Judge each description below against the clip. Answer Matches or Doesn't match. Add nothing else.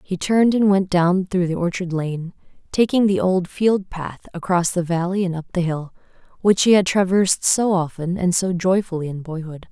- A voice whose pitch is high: Doesn't match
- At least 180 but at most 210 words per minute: Matches